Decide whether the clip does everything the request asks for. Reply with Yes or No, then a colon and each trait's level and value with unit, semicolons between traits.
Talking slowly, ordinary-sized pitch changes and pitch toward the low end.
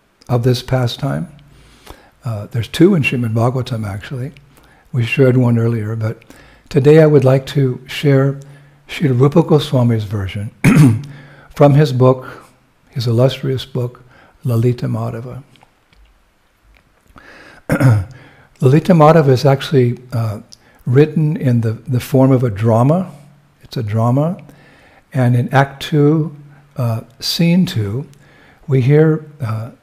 Yes: slow, 115 wpm; average, 3.3 semitones; low, 130 Hz